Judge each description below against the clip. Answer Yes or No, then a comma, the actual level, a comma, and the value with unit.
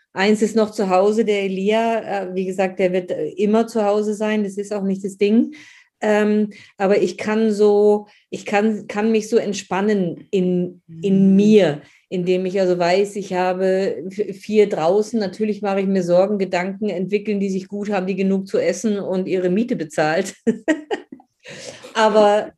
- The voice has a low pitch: No, high, 205 Hz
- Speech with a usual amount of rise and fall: No, narrow, 2.0 semitones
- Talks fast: No, average, 165 wpm